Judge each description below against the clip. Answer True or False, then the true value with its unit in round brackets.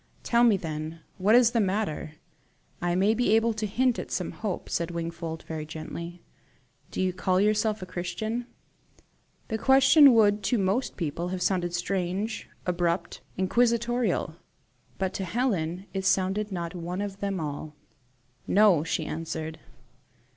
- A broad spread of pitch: False (4.3 semitones)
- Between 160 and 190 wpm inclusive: False (145 wpm)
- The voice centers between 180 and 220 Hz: True (190 Hz)